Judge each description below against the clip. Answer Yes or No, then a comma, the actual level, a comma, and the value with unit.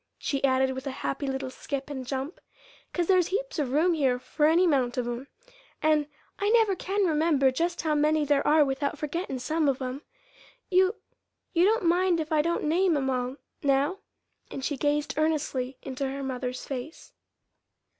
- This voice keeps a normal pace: Yes, average, 180 wpm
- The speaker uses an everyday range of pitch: Yes, average, 4.0 semitones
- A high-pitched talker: Yes, very high, 295 Hz